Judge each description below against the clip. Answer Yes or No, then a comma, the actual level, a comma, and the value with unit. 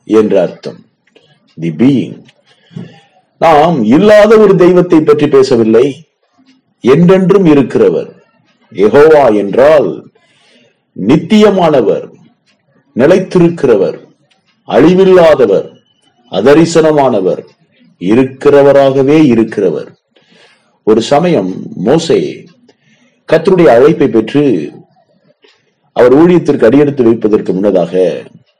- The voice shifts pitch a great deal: Yes, wide, 6.5 semitones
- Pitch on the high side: No, medium, 160 Hz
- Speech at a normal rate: No, slow, 65 wpm